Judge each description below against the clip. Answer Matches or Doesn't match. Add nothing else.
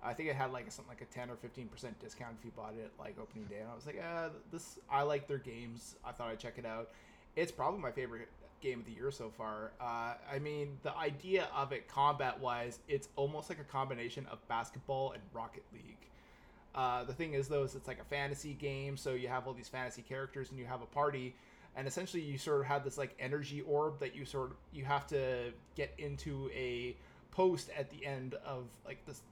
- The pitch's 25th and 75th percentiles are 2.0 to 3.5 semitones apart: Matches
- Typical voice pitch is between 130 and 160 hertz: Matches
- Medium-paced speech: Doesn't match